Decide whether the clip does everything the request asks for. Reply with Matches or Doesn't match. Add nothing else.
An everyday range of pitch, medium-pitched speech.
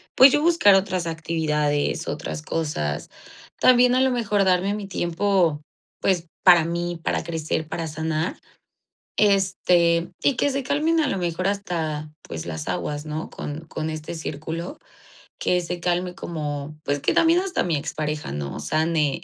Matches